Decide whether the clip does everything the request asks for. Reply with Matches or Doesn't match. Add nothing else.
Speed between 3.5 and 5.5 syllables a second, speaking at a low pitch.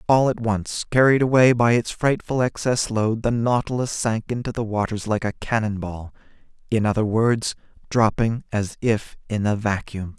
Matches